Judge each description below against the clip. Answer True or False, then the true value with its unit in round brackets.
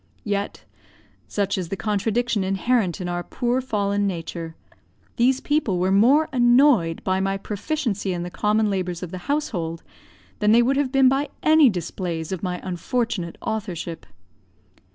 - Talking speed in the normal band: True (155 wpm)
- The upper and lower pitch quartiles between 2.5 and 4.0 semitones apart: False (5.3 semitones)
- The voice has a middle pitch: False (200 Hz)